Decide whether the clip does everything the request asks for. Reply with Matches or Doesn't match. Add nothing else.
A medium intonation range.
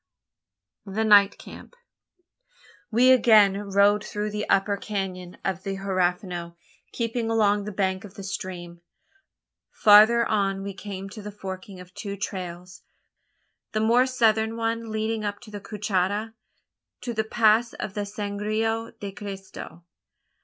Doesn't match